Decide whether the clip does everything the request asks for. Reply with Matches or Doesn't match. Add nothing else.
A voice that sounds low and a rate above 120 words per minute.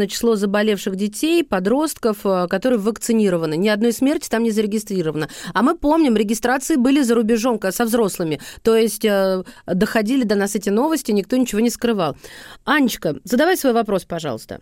Doesn't match